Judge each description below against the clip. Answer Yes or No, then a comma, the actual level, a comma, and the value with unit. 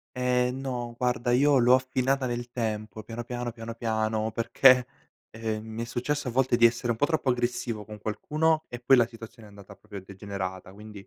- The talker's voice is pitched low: Yes, low, 120 Hz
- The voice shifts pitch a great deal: No, narrow, 2.5 semitones